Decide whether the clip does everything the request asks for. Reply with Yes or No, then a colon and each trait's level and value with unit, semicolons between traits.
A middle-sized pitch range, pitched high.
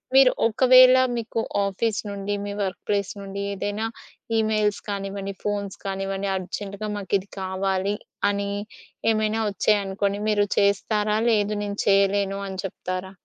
No: narrow, 1.3 semitones; high, 200 Hz